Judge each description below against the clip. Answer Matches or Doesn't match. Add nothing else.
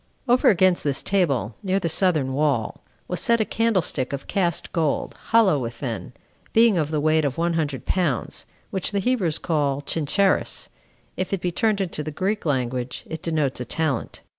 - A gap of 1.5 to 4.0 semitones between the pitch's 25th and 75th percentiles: Doesn't match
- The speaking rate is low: Doesn't match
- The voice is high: Doesn't match